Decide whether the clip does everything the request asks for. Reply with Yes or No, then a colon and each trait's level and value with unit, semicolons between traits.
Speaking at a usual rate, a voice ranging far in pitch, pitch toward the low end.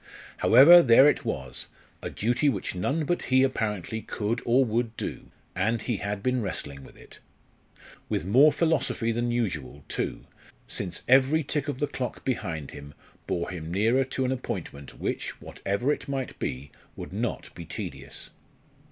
Yes: average, 160 wpm; wide, 6.2 semitones; low, 115 Hz